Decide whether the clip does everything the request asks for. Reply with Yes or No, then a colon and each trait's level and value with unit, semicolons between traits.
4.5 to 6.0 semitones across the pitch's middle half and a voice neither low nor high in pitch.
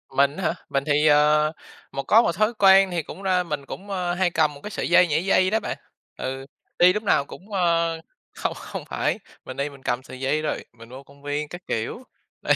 Yes: average, 4.9 semitones; medium, 155 Hz